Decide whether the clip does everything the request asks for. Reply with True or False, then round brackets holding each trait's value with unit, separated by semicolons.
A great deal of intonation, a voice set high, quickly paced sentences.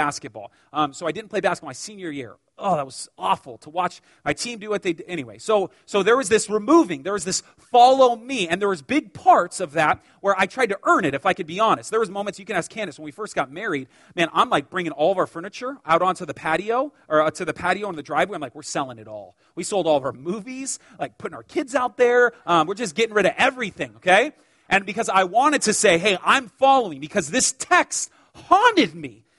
True (6.3 semitones; 205 Hz; 250 wpm)